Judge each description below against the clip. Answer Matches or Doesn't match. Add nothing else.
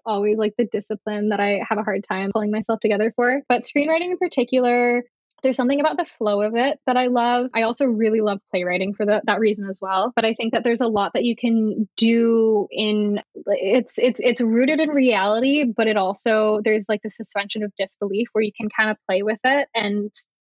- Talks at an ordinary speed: Doesn't match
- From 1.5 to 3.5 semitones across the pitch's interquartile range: Matches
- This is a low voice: Doesn't match